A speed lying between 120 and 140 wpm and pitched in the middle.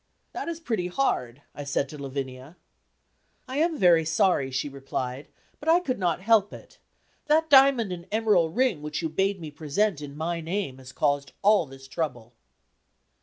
No: average, 170 wpm; medium, 165 Hz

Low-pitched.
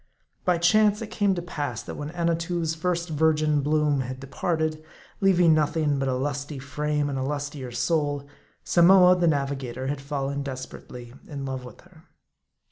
No: medium, 150 Hz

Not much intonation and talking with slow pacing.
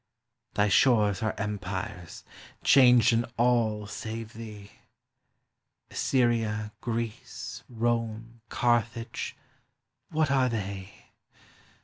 Yes: narrow, 2.1 semitones; slow, 80 wpm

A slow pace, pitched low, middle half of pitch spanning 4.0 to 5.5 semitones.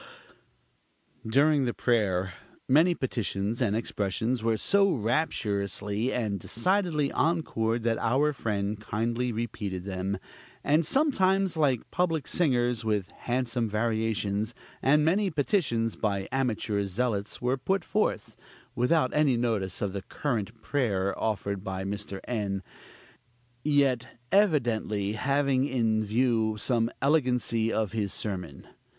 Yes: slow, 120 wpm; low, 115 Hz; average, 5.0 semitones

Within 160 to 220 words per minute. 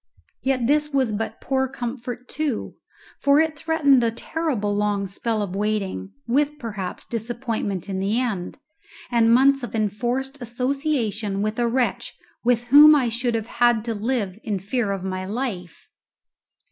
No: average, 145 wpm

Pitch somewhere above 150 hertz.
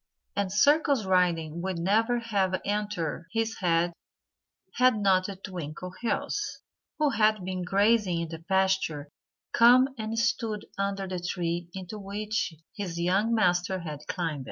Yes: high, 190 Hz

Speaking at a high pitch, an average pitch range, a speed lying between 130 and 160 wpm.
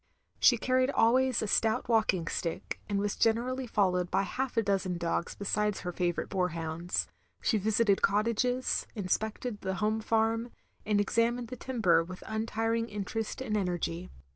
Yes: high, 215 Hz; average, 3.7 semitones; average, 150 wpm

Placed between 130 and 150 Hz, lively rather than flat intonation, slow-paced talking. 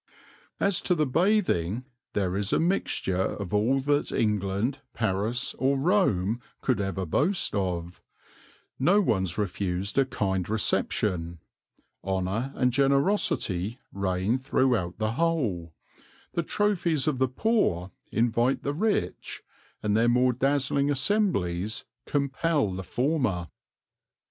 No: low, 120 Hz; wide, 7.0 semitones; slow, 120 wpm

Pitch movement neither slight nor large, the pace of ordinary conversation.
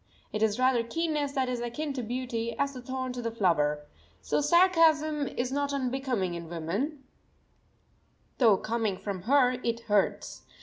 Yes: average, 4.6 semitones; average, 160 wpm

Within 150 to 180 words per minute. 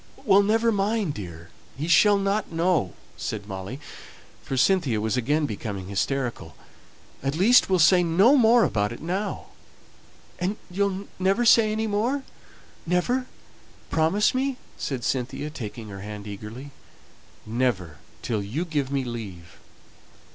No: slow, 135 wpm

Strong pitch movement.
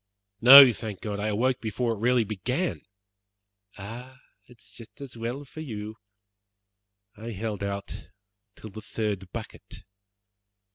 No: average, 3.2 semitones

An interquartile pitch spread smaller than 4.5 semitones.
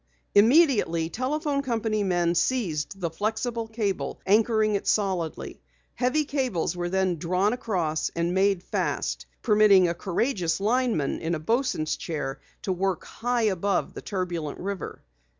No: average, 4.9 semitones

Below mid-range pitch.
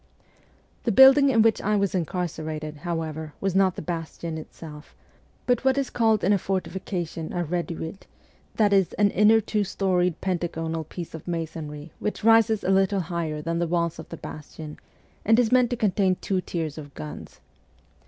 No: medium, 175 Hz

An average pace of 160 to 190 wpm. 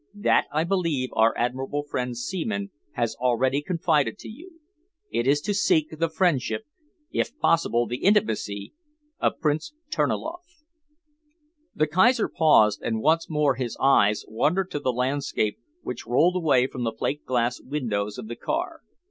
No: average, 150 wpm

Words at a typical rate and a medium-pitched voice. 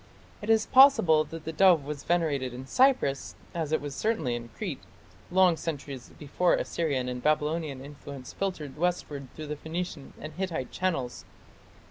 Yes: average, 150 wpm; medium, 155 Hz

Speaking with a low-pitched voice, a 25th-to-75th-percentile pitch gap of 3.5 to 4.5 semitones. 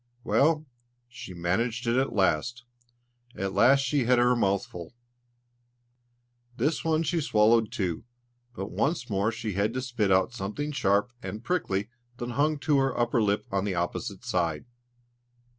No: low, 115 Hz; average, 4.9 semitones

